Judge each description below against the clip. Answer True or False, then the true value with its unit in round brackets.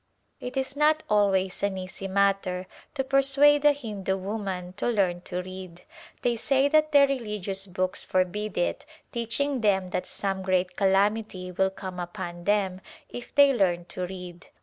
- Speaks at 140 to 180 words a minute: True (165 wpm)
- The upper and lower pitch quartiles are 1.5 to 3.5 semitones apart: False (4.7 semitones)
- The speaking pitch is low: False (195 Hz)